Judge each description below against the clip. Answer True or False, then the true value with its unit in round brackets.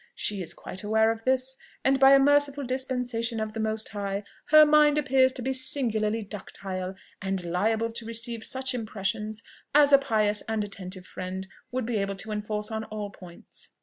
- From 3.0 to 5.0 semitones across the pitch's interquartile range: True (4.0 semitones)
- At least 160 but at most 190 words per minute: True (180 wpm)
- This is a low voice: False (220 Hz)